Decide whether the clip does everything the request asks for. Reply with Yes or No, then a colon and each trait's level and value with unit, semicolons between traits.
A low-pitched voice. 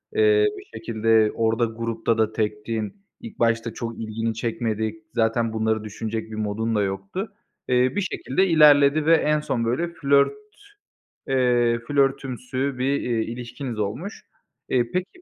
Yes: low, 120 Hz